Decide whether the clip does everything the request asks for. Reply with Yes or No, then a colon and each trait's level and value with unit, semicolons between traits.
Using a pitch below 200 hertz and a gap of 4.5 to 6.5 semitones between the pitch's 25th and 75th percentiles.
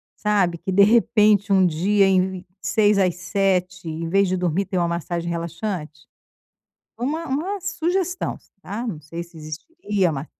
No: high, 190 Hz; average, 3.8 semitones